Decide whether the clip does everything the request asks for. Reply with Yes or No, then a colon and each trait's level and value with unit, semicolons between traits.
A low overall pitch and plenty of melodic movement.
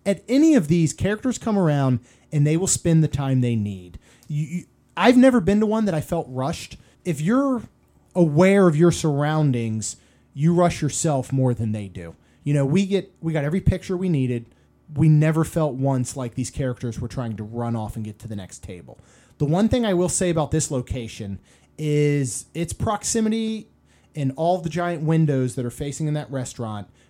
No: medium, 150 Hz; wide, 6.3 semitones